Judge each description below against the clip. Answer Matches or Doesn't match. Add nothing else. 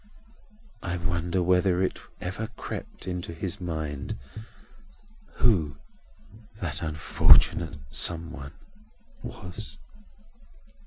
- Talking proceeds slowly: Matches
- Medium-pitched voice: Doesn't match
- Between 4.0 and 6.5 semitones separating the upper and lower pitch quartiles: Doesn't match